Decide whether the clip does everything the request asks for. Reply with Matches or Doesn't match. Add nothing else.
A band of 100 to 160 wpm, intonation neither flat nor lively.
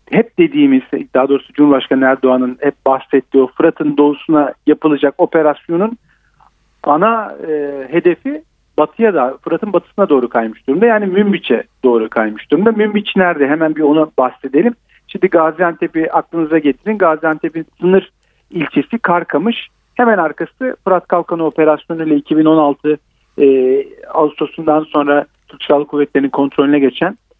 Matches